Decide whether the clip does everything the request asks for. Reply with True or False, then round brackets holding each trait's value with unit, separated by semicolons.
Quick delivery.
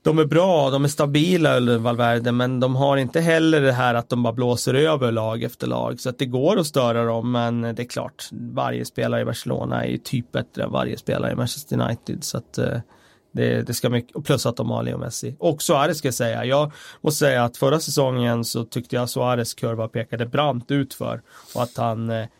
True (230 wpm)